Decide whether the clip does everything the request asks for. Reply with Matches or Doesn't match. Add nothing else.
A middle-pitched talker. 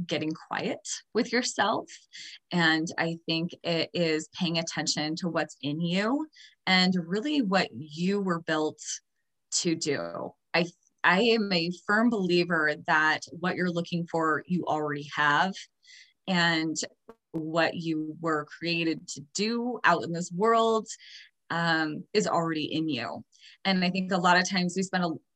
Matches